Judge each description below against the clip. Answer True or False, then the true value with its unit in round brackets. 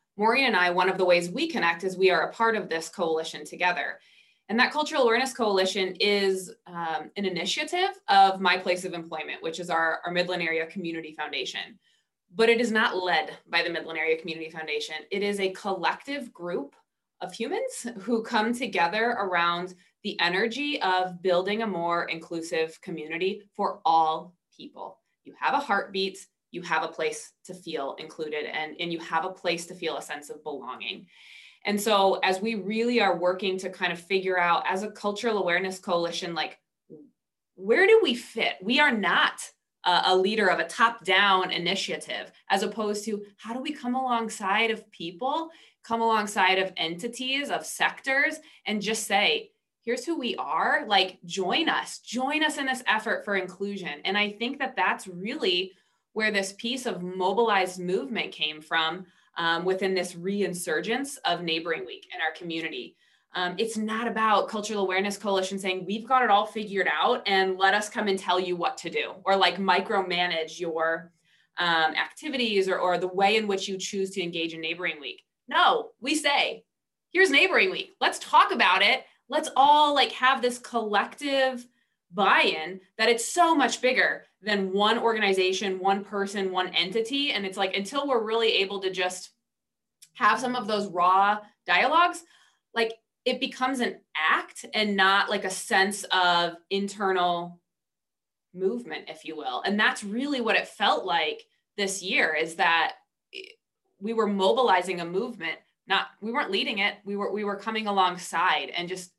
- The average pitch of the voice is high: True (195 Hz)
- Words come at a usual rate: True (175 wpm)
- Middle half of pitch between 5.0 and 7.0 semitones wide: False (4.4 semitones)